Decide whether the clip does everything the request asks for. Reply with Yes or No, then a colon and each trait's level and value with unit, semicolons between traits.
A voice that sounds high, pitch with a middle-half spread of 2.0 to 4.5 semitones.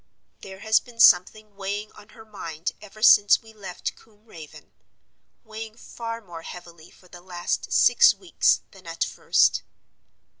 Yes: high, 205 Hz; average, 3.7 semitones